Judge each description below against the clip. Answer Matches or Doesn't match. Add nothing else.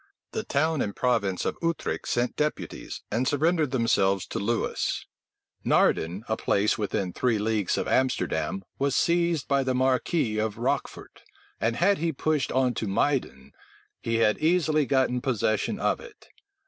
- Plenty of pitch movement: Matches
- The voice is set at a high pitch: Doesn't match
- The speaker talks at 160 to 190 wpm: Doesn't match